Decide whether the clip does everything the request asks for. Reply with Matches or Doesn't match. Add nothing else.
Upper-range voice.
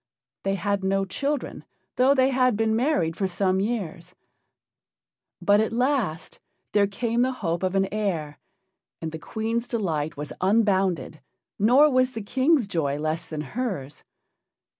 Matches